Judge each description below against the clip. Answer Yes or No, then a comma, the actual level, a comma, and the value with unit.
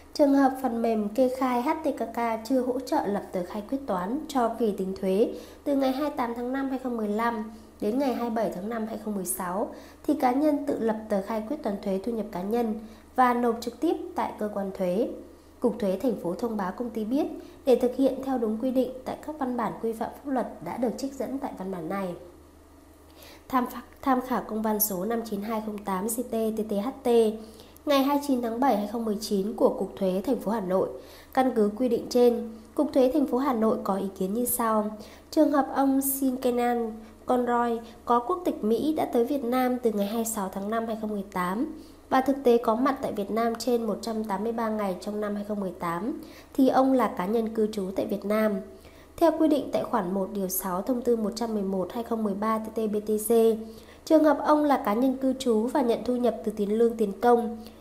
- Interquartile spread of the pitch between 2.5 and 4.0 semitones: Yes, average, 3.6 semitones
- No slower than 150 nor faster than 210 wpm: Yes, average, 205 wpm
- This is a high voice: Yes, high, 230 Hz